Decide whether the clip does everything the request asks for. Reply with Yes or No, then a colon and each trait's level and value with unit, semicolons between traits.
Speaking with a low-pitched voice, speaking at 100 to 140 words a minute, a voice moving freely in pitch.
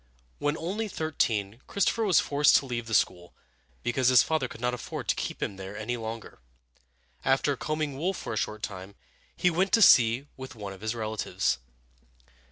No: low, 120 Hz; average, 175 wpm; wide, 6.1 semitones